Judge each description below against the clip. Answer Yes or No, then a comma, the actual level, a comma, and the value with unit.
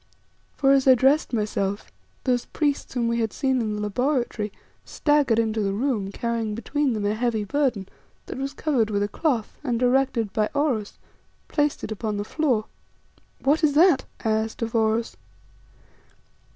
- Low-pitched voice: No, high, 235 Hz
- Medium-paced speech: Yes, average, 165 wpm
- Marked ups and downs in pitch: No, average, 4.1 semitones